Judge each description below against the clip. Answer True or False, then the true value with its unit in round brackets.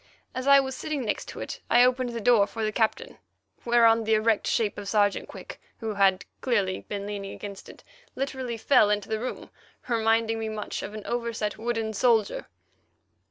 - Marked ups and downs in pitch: False (2.5 semitones)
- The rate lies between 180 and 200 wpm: True (185 wpm)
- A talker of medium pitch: False (225 Hz)